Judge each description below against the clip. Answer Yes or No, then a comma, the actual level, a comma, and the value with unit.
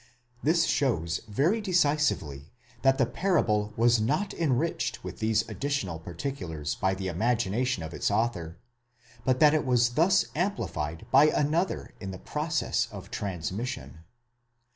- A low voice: Yes, low, 120 Hz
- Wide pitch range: Yes, wide, 7.9 semitones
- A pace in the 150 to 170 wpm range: No, average, 140 wpm